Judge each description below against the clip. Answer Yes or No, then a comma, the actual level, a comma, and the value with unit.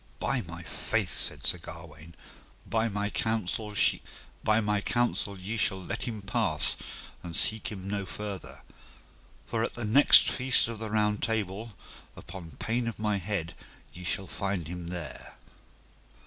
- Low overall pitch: Yes, low, 105 Hz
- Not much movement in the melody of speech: No, average, 3.5 semitones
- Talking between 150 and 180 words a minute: No, average, 140 wpm